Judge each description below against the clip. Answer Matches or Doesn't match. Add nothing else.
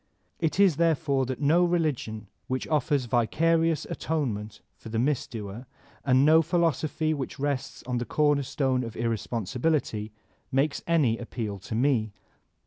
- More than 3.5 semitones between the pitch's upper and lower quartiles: Matches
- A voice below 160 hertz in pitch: Matches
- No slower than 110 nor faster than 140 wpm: Matches